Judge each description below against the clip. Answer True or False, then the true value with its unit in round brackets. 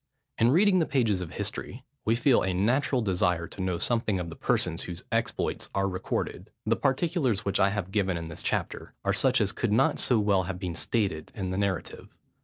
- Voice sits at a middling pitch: False (100 Hz)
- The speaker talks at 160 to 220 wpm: True (205 wpm)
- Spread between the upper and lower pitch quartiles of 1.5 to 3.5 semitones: False (4.4 semitones)